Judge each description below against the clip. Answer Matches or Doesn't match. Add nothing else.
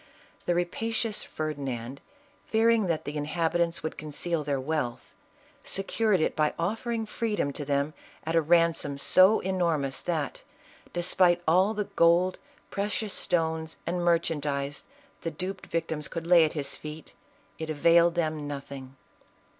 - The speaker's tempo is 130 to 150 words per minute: Matches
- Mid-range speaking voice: Matches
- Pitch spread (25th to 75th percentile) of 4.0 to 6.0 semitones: Doesn't match